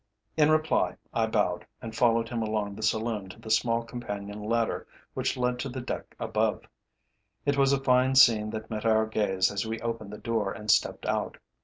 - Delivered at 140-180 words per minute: No, average, 195 wpm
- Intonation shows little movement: Yes, narrow, 2.3 semitones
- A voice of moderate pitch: No, low, 115 Hz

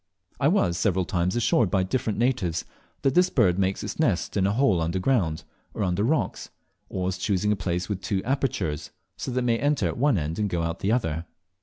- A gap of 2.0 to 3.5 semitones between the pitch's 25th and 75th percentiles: No, average, 5.3 semitones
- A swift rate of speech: Yes, fast, 215 wpm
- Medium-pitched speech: No, very low, 95 Hz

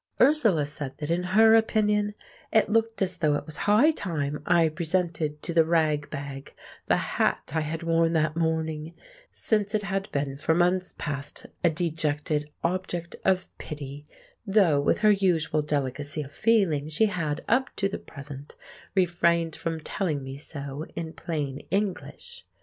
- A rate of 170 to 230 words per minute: No, average, 155 wpm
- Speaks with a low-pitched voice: No, medium, 165 Hz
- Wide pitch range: No, average, 4.4 semitones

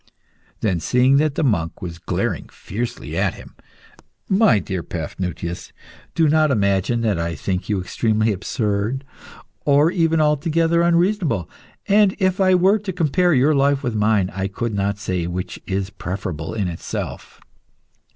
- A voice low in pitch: Yes, low, 115 Hz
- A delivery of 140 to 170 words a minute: Yes, average, 150 wpm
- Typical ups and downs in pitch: No, wide, 8.7 semitones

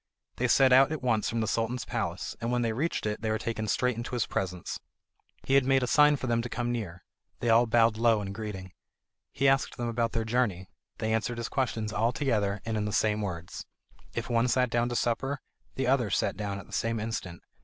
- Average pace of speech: No, fast, 230 wpm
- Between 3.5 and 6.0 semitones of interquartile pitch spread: No, narrow, 2.6 semitones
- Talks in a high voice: No, low, 115 Hz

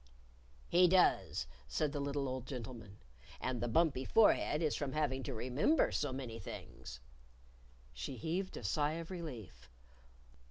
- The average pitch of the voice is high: No, low, 135 Hz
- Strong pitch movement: No, average, 4.6 semitones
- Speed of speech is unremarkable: Yes, average, 145 wpm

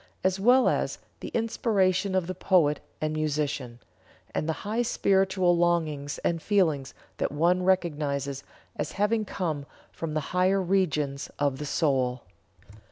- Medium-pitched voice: Yes, medium, 170 Hz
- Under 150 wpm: Yes, average, 140 wpm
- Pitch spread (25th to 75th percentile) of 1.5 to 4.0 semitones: No, average, 4.5 semitones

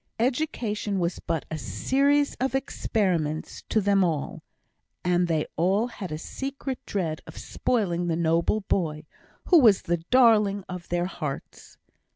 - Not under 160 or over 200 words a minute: No, average, 145 wpm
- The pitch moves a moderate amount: No, wide, 5.8 semitones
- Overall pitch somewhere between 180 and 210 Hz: Yes, high, 190 Hz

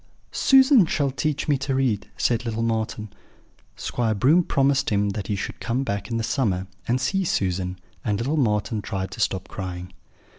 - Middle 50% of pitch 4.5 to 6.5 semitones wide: Yes, average, 5.3 semitones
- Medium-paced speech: Yes, average, 180 wpm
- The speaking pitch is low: Yes, low, 115 Hz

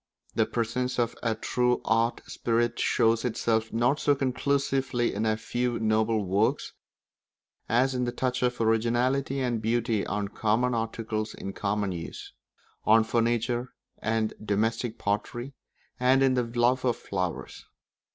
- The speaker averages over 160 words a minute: No, average, 140 wpm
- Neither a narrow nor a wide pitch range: No, narrow, 2.1 semitones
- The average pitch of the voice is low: Yes, low, 115 Hz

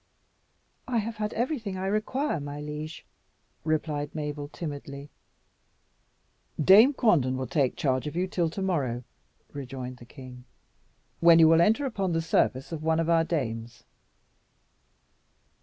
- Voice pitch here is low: No, medium, 155 Hz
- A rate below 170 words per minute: Yes, average, 140 wpm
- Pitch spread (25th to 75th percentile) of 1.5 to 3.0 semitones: No, average, 5.3 semitones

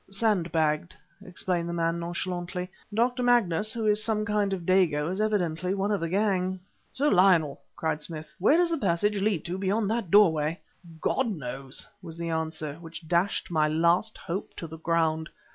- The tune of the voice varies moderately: Yes, average, 4.1 semitones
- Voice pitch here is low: No, medium, 180 Hz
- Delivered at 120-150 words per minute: No, average, 175 wpm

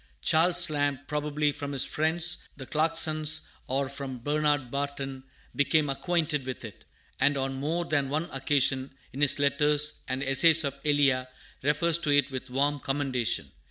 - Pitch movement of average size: No, narrow, 2.2 semitones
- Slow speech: No, average, 155 wpm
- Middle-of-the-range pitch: Yes, medium, 145 Hz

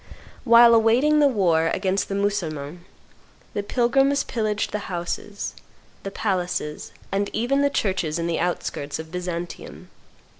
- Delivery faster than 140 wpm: No, slow, 135 wpm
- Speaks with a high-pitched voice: Yes, high, 200 Hz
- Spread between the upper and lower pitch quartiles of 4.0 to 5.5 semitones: Yes, average, 5.1 semitones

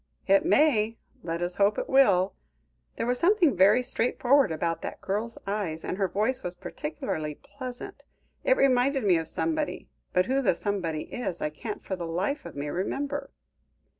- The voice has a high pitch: Yes, high, 205 Hz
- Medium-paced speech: Yes, average, 170 wpm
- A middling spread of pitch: No, wide, 6.8 semitones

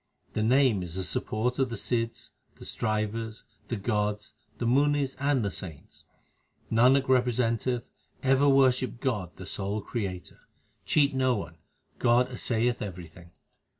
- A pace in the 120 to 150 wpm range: Yes, slow, 135 wpm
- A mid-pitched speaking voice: No, low, 115 Hz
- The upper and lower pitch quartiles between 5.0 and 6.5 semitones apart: No, average, 3.9 semitones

